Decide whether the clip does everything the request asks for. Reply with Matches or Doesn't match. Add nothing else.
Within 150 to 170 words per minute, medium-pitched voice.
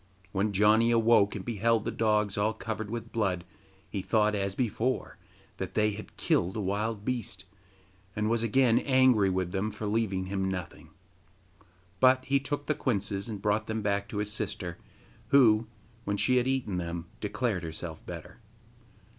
Doesn't match